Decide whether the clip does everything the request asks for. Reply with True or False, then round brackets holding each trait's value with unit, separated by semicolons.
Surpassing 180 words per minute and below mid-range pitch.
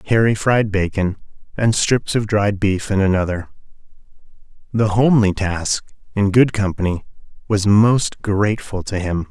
False (135 wpm; 100 Hz)